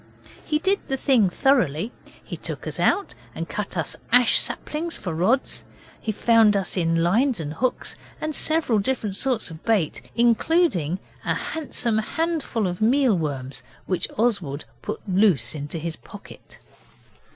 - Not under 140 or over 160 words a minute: Yes, average, 150 wpm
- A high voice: Yes, high, 215 Hz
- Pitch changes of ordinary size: No, wide, 7.8 semitones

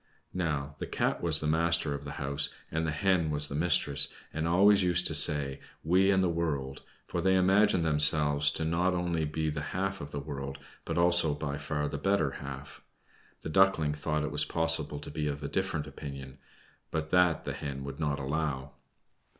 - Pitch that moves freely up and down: No, average, 3.0 semitones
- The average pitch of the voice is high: No, very low, 75 Hz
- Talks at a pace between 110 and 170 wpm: No, average, 195 wpm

